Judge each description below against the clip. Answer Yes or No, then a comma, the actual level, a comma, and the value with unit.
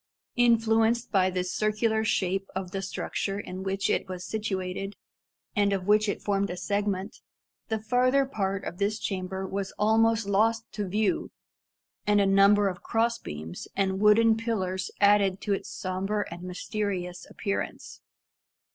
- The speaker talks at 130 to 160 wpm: Yes, average, 150 wpm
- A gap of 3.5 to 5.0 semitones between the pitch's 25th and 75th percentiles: No, narrow, 2.4 semitones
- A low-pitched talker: No, high, 200 Hz